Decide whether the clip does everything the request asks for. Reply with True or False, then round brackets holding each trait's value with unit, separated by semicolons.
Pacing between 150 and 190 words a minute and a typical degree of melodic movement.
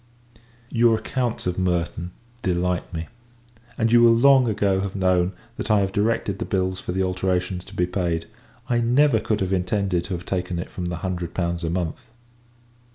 True (185 wpm; 3.3 semitones)